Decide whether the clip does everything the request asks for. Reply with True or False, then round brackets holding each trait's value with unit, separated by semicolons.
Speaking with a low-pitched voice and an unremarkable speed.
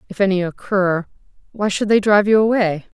False (195 Hz; 180 wpm)